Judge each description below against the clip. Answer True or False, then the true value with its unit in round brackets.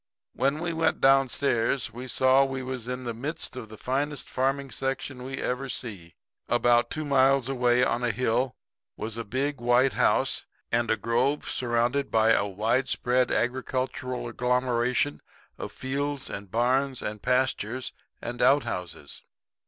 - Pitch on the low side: True (125 Hz)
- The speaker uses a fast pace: False (155 wpm)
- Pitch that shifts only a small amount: True (2.2 semitones)